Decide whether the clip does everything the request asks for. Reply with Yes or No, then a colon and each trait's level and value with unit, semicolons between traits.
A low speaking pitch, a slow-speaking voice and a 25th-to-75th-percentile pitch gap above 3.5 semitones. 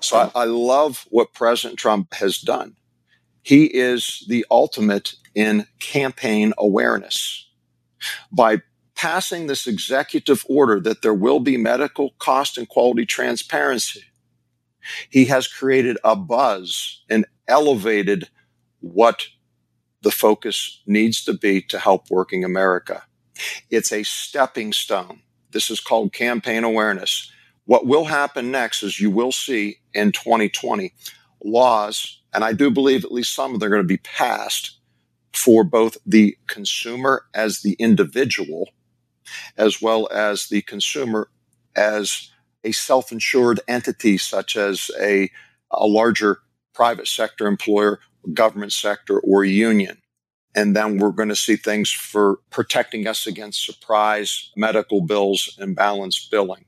No: low, 105 Hz; slow, 130 wpm; average, 3.1 semitones